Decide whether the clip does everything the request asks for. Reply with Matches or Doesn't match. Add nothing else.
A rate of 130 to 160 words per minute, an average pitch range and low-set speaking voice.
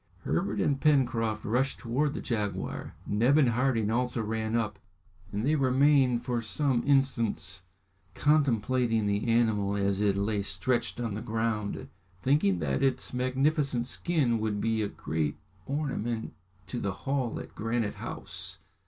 Matches